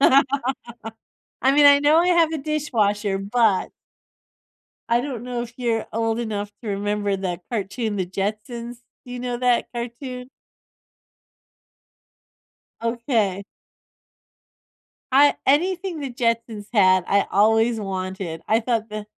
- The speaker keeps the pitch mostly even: No, average, 3.7 semitones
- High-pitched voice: Yes, high, 230 Hz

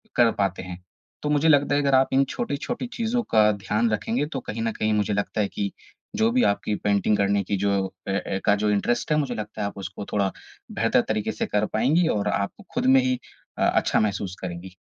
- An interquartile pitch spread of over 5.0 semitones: Yes, wide, 5.4 semitones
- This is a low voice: Yes, low, 105 Hz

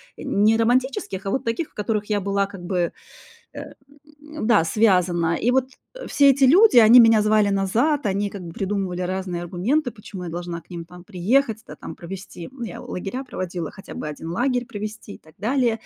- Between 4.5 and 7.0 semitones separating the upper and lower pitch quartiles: Yes, average, 5.1 semitones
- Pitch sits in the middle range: No, high, 205 Hz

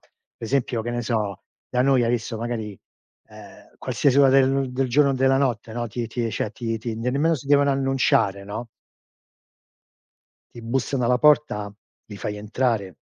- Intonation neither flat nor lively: Yes, average, 3.1 semitones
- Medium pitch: No, low, 120 Hz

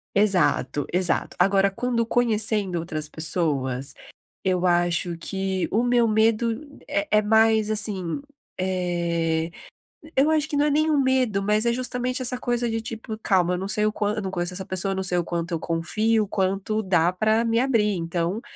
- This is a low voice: No, high, 200 Hz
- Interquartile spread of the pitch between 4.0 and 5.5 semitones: Yes, average, 4.4 semitones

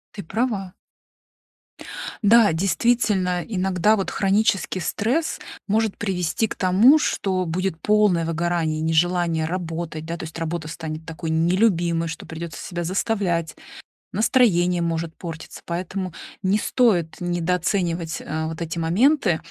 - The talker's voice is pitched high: No, medium, 175 Hz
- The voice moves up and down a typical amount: Yes, average, 3.4 semitones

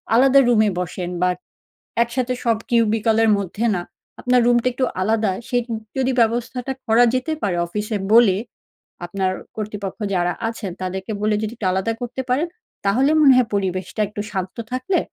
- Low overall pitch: No, high, 225 Hz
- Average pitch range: Yes, average, 4.0 semitones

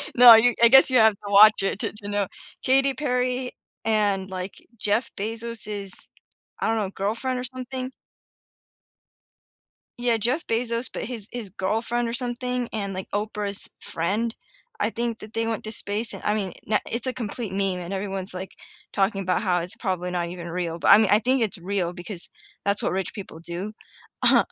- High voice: Yes, high, 215 Hz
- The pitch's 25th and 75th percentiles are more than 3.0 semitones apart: Yes, average, 3.6 semitones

